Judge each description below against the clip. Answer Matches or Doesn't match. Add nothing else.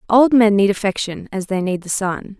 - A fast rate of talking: Matches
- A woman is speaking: Matches